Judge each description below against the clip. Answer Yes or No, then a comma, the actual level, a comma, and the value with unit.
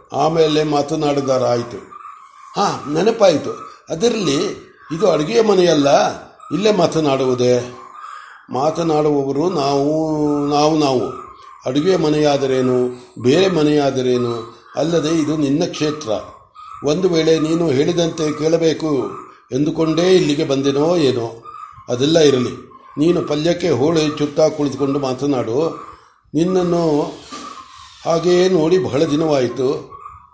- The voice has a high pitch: No, medium, 155 Hz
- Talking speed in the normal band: Yes, average, 85 wpm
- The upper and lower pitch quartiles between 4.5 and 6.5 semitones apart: No, average, 3.0 semitones